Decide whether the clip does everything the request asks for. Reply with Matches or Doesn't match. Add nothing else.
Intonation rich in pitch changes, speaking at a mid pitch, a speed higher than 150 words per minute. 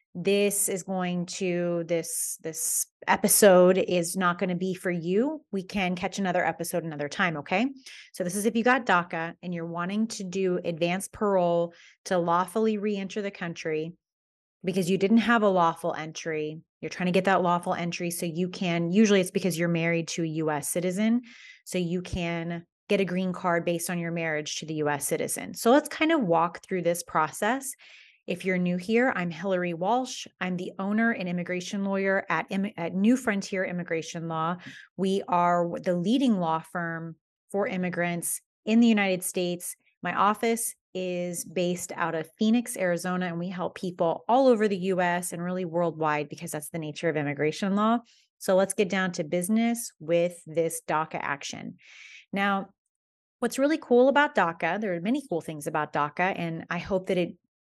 Doesn't match